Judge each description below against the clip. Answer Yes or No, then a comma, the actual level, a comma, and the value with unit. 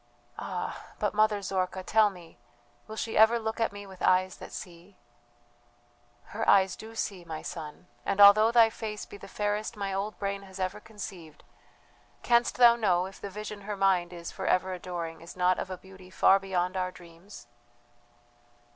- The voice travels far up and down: No, narrow, 2.6 semitones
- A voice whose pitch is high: Yes, high, 195 Hz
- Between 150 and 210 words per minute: Yes, average, 180 wpm